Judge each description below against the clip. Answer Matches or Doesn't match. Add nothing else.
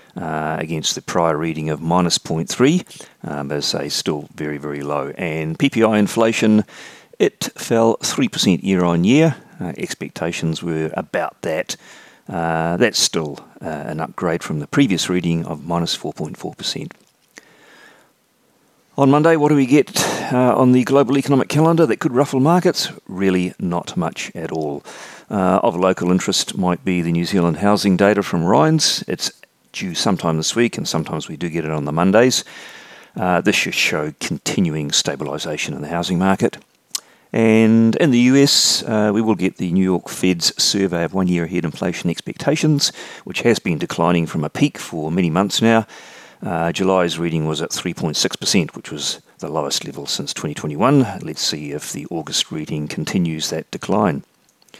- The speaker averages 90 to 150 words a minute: Doesn't match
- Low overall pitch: Matches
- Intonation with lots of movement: Matches